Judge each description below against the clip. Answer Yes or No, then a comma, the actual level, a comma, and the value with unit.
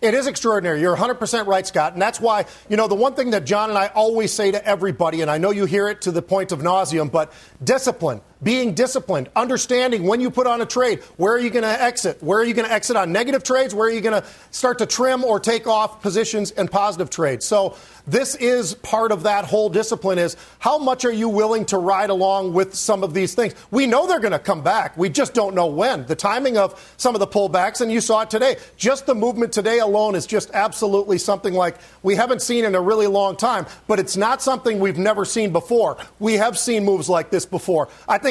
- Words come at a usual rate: No, fast, 245 wpm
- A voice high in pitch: Yes, high, 210 Hz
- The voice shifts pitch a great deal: No, average, 3.5 semitones